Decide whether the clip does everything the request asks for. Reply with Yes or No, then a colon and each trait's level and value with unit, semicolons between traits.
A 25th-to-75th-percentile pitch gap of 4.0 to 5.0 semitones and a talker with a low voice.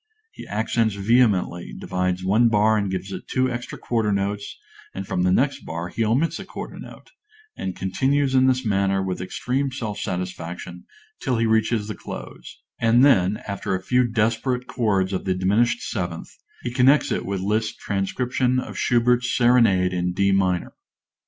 Yes: average, 4.6 semitones; low, 105 Hz